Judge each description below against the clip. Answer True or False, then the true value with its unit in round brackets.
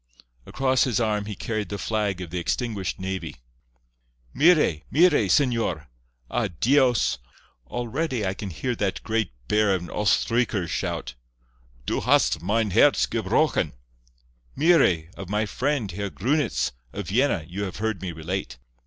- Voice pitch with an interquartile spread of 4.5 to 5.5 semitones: True (4.9 semitones)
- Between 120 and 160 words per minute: True (145 wpm)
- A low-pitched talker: True (105 Hz)